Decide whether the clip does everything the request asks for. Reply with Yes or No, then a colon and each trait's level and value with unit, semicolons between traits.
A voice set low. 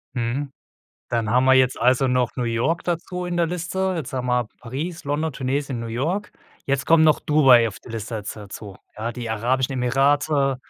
Yes: low, 130 Hz